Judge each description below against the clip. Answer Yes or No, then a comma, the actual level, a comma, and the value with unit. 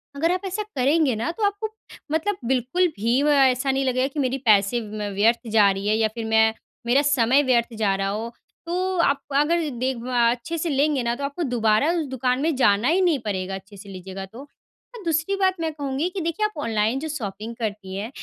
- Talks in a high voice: Yes, very high, 255 Hz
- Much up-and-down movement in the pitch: Yes, wide, 6.1 semitones